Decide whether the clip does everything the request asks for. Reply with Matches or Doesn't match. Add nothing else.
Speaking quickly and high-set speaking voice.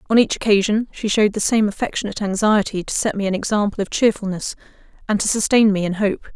Matches